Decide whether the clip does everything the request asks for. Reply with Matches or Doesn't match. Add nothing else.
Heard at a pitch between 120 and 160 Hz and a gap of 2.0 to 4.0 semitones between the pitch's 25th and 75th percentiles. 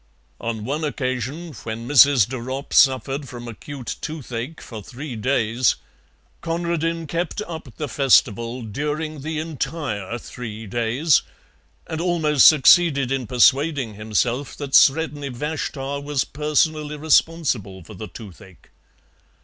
Doesn't match